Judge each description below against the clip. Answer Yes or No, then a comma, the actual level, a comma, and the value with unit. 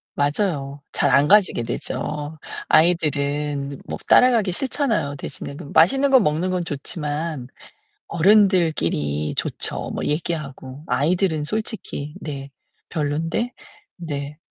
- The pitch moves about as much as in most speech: Yes, average, 4.4 semitones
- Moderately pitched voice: Yes, medium, 155 Hz